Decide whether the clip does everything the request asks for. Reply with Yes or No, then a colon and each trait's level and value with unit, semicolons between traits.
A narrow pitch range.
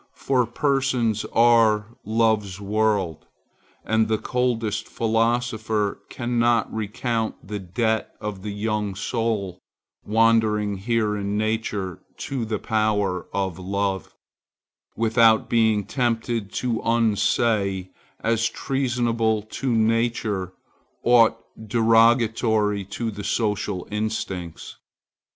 Yes: narrow, 2.1 semitones